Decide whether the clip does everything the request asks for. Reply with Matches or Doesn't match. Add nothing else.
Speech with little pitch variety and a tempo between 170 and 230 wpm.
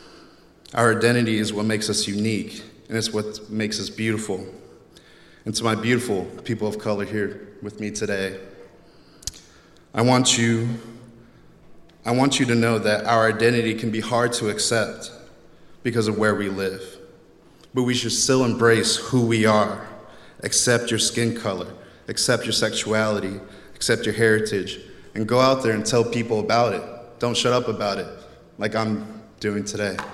Doesn't match